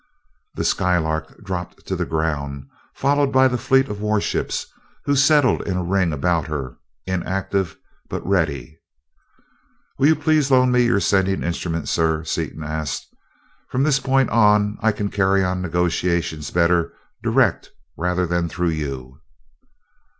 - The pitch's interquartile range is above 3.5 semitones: Yes, average, 5.0 semitones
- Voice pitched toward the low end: Yes, very low, 90 Hz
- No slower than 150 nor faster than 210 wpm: No, average, 140 wpm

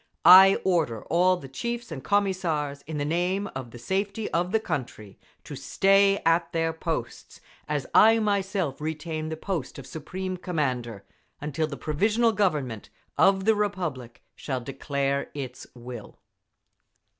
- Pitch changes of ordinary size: No, wide, 5.8 semitones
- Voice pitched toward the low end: No, medium, 160 Hz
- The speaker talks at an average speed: Yes, average, 145 wpm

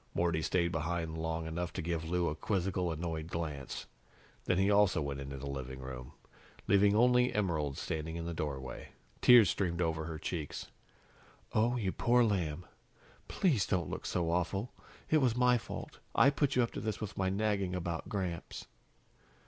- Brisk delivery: No, average, 175 wpm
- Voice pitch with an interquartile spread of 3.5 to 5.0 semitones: Yes, average, 4.3 semitones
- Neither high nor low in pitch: No, very low, 85 Hz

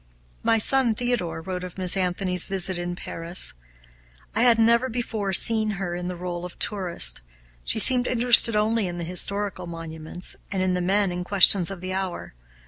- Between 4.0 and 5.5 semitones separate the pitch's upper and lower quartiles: No, average, 3.5 semitones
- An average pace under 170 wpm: No, average, 175 wpm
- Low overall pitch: No, medium, 185 Hz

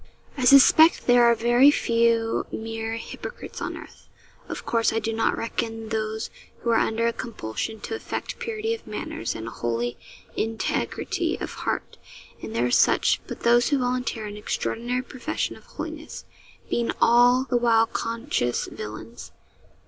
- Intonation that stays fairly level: Yes, narrow, 2.0 semitones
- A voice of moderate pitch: No, high, 230 Hz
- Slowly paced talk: No, average, 155 wpm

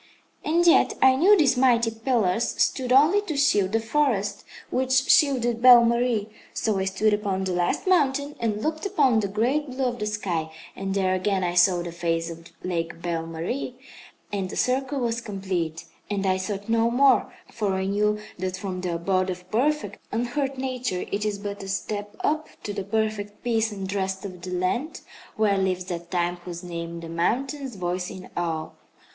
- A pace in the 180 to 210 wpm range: Yes, average, 185 wpm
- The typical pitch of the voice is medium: No, high, 205 Hz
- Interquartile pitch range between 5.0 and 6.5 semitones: Yes, wide, 5.4 semitones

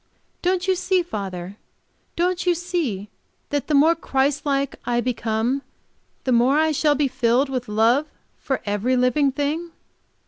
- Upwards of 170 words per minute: No, average, 150 wpm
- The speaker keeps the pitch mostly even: No, average, 4.9 semitones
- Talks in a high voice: Yes, very high, 275 Hz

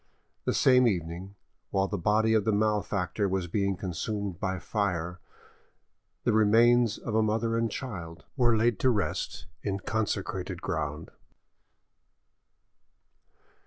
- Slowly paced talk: Yes, slow, 125 wpm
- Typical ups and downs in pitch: Yes, average, 3.1 semitones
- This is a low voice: Yes, low, 105 Hz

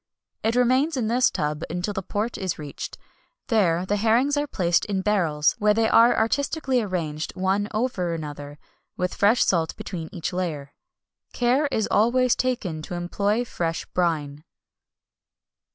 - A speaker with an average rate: Yes, average, 150 wpm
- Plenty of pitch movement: Yes, wide, 6.0 semitones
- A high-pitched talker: Yes, high, 200 Hz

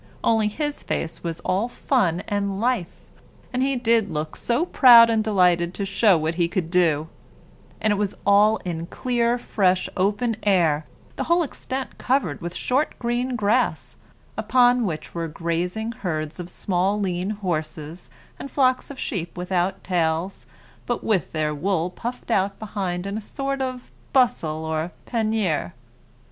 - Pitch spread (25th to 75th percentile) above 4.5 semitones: Yes, wide, 5.6 semitones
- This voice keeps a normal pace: Yes, average, 155 wpm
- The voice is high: Yes, high, 200 Hz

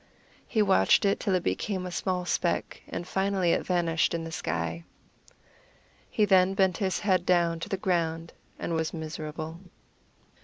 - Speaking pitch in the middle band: Yes, medium, 175 Hz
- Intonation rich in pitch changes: No, average, 2.7 semitones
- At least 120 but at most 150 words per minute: No, average, 160 wpm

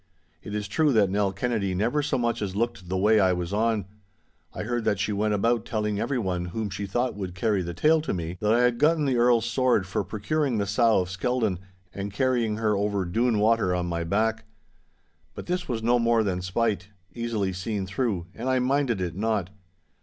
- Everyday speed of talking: No, fast, 210 wpm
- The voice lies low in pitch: Yes, low, 110 Hz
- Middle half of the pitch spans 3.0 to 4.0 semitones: Yes, average, 3.6 semitones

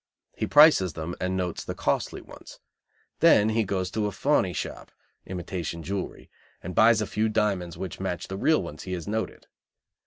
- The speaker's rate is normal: Yes, average, 180 wpm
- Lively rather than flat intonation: No, average, 3.3 semitones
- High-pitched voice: No, very low, 95 Hz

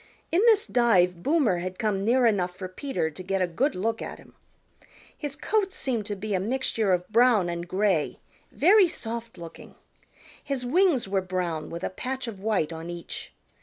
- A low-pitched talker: No, high, 210 Hz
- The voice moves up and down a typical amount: No, wide, 6.1 semitones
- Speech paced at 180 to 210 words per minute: Yes, average, 185 wpm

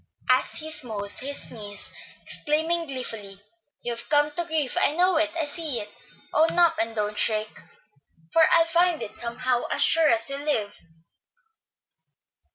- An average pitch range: No, wide, 6.2 semitones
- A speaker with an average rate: Yes, average, 160 wpm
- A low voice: No, very high, 285 Hz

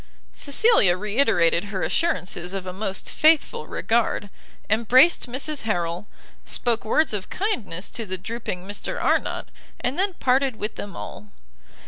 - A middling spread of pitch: No, wide, 6.5 semitones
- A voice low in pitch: No, high, 215 Hz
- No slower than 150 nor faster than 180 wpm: No, average, 140 wpm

